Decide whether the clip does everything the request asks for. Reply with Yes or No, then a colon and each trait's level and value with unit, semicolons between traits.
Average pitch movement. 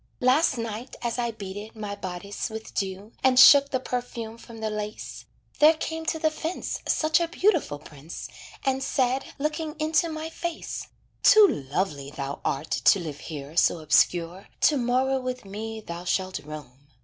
No: wide, 7.6 semitones